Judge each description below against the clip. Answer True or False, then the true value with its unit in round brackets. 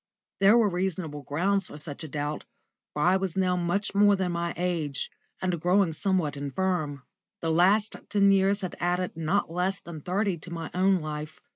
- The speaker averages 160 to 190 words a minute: True (180 wpm)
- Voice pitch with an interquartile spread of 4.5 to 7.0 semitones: False (3.4 semitones)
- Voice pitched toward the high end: False (180 Hz)